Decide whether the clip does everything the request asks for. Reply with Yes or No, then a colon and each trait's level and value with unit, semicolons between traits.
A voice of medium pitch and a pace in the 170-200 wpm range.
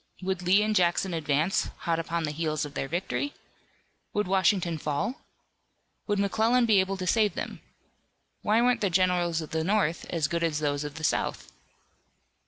Yes: medium, 175 Hz; average, 175 wpm